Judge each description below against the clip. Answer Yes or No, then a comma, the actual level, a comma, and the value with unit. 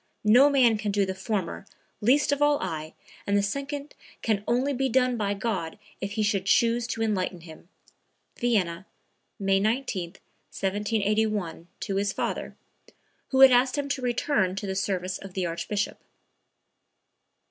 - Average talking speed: Yes, average, 155 wpm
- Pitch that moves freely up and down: No, average, 4.3 semitones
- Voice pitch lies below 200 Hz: No, high, 210 Hz